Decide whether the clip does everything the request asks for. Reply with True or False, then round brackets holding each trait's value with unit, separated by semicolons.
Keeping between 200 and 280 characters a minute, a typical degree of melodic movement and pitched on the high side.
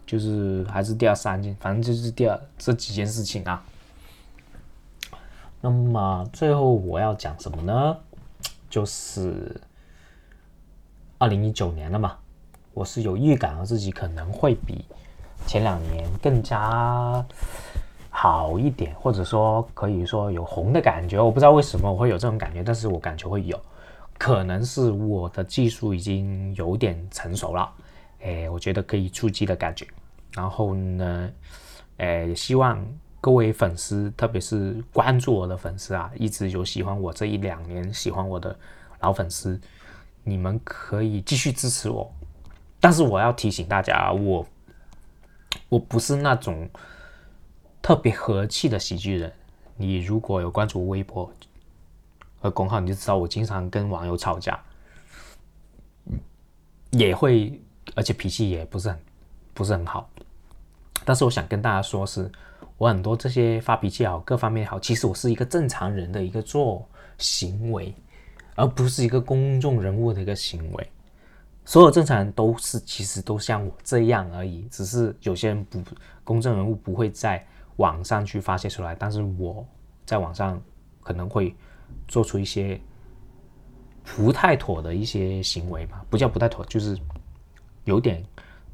False (235 characters per minute; 4.2 semitones; 100 Hz)